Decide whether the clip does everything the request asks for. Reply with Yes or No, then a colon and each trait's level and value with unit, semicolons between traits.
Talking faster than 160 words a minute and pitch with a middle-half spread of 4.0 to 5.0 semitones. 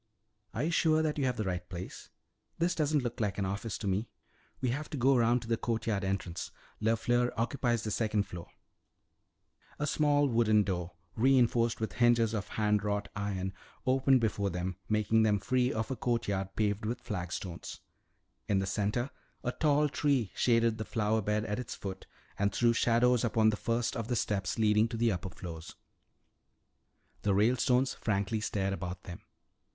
No: average, 175 wpm; average, 3.3 semitones